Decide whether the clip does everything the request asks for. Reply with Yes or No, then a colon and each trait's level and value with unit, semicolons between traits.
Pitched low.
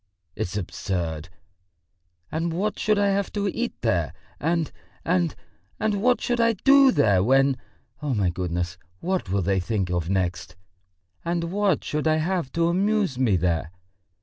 No: medium, 155 Hz